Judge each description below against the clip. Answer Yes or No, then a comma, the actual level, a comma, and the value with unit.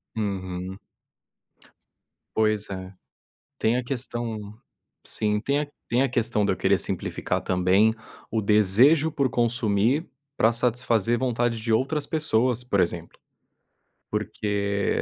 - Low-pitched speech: Yes, low, 110 Hz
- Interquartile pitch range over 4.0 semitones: No, average, 3.5 semitones